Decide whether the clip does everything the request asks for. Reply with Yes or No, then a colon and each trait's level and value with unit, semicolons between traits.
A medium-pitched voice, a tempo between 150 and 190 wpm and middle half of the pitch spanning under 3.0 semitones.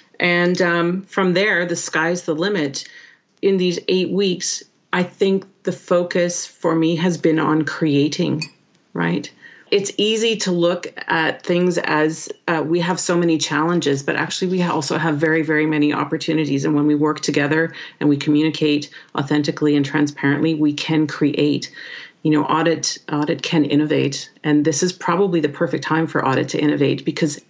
Yes: medium, 160 Hz; average, 170 wpm; narrow, 2.5 semitones